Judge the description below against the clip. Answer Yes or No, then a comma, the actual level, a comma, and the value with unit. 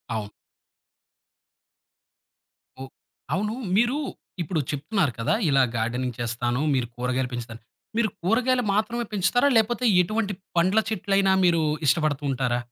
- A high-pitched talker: No, medium, 170 Hz